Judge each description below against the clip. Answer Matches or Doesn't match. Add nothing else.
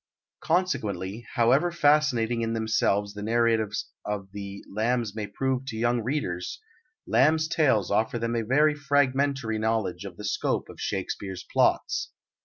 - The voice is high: Doesn't match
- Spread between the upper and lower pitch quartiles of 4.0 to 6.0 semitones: Matches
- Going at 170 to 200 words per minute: Doesn't match